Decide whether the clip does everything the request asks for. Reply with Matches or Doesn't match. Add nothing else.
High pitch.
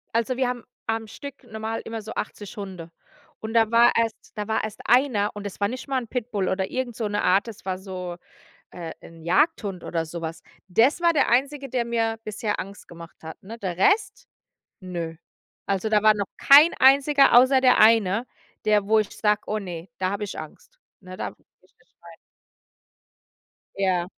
Matches